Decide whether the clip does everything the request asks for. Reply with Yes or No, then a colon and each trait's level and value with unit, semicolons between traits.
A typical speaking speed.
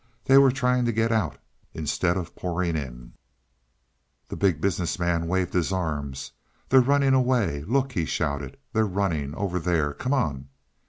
Yes: average, 160 wpm